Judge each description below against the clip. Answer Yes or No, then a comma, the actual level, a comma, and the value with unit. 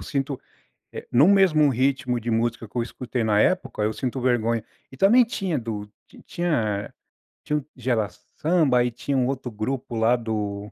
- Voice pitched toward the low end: Yes, low, 125 Hz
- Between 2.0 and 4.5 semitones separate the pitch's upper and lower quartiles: Yes, average, 3.7 semitones